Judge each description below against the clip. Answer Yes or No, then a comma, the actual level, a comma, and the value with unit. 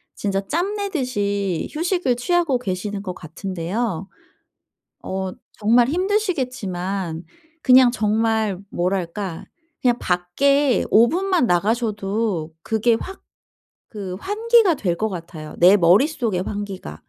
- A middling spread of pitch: No, wide, 6.1 semitones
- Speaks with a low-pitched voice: No, high, 210 Hz